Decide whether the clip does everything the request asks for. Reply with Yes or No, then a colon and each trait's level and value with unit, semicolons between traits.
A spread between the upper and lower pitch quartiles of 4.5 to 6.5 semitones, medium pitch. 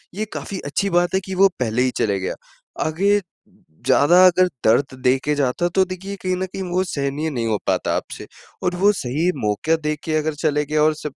Yes: average, 4.9 semitones; medium, 155 Hz